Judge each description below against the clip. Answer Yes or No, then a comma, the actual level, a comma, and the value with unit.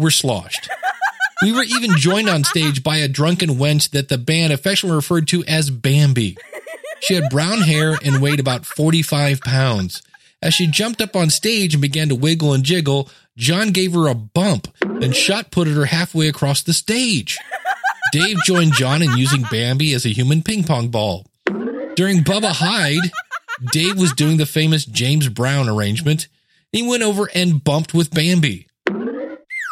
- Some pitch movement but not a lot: Yes, average, 4.8 semitones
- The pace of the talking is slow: No, average, 170 wpm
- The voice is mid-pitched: Yes, medium, 155 Hz